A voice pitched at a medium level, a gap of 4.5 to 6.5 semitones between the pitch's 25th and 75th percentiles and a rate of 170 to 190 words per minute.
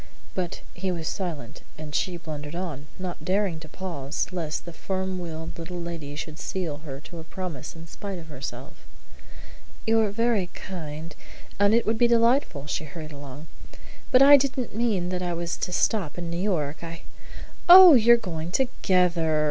No: medium, 175 Hz; average, 4.0 semitones; average, 180 wpm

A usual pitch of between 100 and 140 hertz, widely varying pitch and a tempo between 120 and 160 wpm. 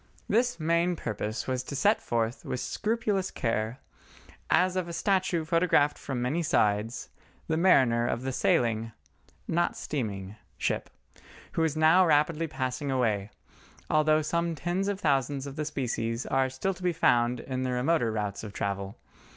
Yes: low, 135 Hz; wide, 6.3 semitones; average, 150 wpm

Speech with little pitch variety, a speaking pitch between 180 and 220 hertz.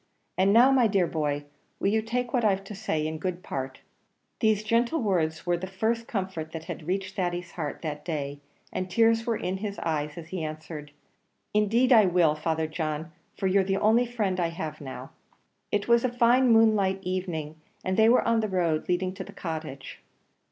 No: wide, 5.5 semitones; medium, 185 Hz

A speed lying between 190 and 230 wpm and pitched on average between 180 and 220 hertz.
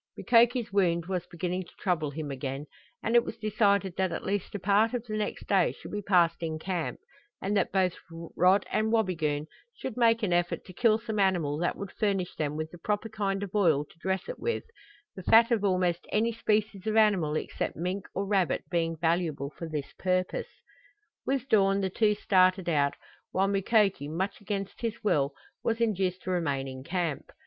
Yes: average, 195 wpm; high, 190 Hz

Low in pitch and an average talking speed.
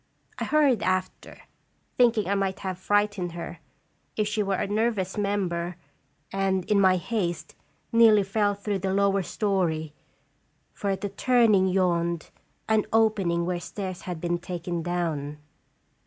No: high, 195 Hz; average, 150 wpm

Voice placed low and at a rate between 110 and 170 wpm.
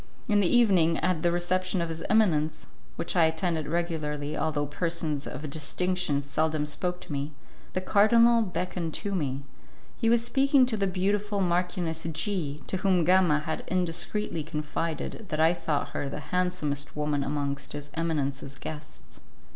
No: medium, 165 Hz; average, 155 wpm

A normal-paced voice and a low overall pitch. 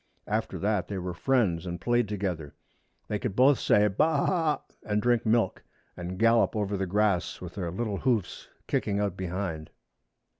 Yes: average, 175 wpm; low, 100 Hz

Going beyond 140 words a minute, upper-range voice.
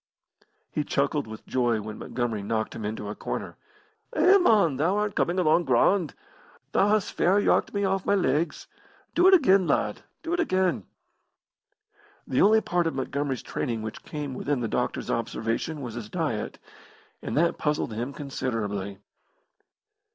No: average, 160 wpm; medium, 145 Hz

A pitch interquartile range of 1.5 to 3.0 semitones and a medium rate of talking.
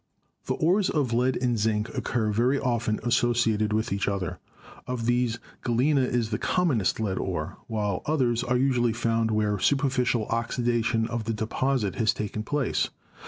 Yes: narrow, 2.6 semitones; average, 165 wpm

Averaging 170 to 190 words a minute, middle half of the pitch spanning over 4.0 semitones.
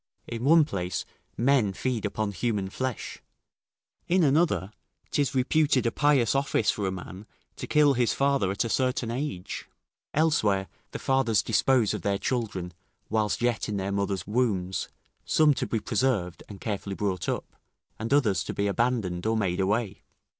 No: average, 160 wpm; average, 5.0 semitones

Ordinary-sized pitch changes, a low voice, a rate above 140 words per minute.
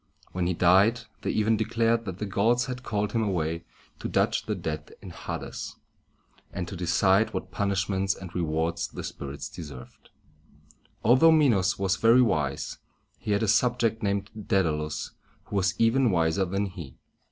Yes: average, 4.4 semitones; very low, 95 Hz; average, 165 wpm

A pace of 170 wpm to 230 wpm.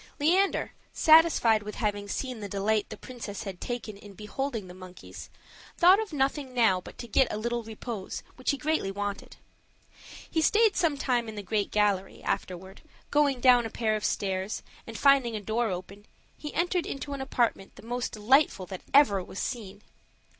Yes: average, 175 wpm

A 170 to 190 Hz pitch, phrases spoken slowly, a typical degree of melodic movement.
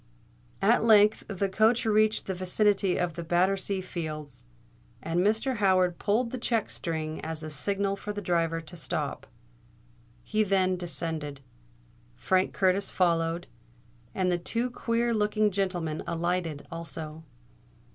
Yes: medium, 185 Hz; slow, 130 wpm; average, 3.9 semitones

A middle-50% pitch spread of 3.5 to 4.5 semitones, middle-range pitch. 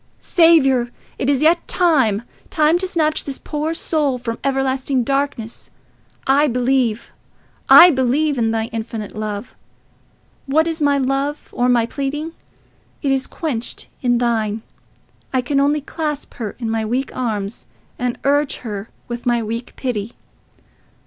No: average, 4.0 semitones; very high, 260 Hz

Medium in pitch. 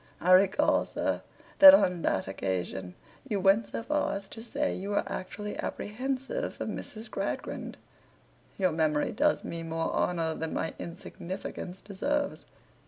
No: high, 195 Hz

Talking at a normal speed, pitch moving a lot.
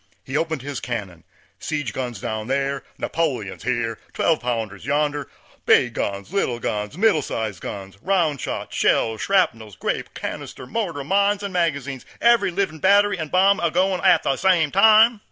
Yes: average, 160 wpm; wide, 8.1 semitones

